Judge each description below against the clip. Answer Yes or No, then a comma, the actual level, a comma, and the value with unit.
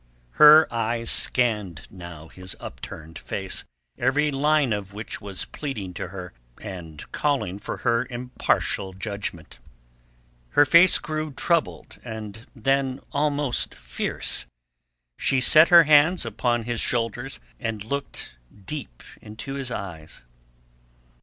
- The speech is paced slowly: Yes, slow, 115 wpm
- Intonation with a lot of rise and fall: Yes, wide, 6.2 semitones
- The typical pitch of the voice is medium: No, low, 115 Hz